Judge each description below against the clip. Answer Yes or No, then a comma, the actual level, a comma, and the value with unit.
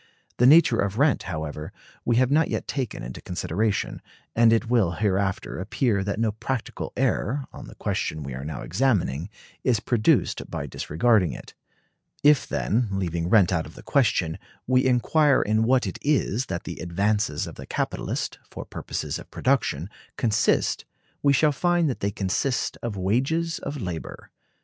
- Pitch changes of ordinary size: No, wide, 6.0 semitones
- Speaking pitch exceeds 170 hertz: No, low, 110 Hz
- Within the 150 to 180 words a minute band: Yes, average, 165 wpm